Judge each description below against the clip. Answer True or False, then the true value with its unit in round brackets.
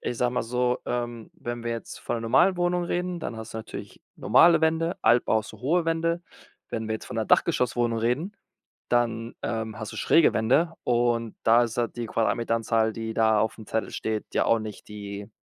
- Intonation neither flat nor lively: False (2.3 semitones)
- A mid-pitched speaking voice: False (115 Hz)